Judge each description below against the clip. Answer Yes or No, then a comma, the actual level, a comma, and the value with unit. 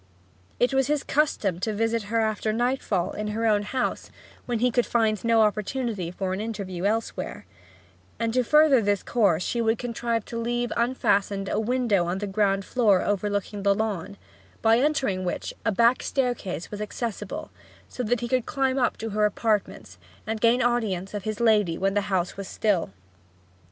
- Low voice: No, high, 220 Hz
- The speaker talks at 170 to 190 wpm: Yes, average, 180 wpm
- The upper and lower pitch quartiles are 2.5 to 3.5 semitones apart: Yes, average, 3.2 semitones